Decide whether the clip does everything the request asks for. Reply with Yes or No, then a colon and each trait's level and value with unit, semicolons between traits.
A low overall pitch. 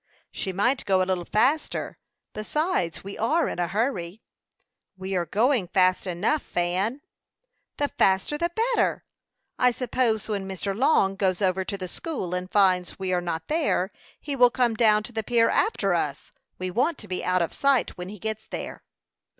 No: high, 205 Hz